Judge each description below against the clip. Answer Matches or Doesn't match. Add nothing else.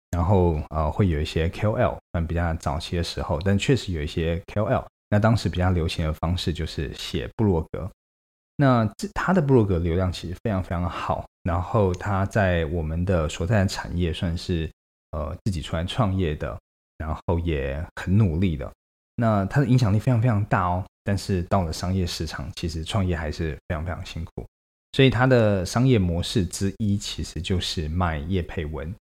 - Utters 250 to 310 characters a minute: Matches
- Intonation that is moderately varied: Matches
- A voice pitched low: Matches